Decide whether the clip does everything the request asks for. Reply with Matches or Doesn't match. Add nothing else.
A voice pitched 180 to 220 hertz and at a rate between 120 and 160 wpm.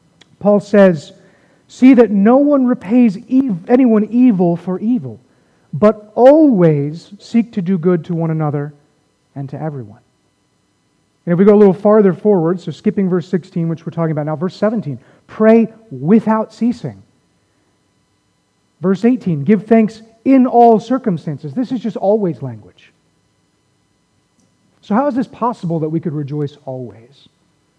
Matches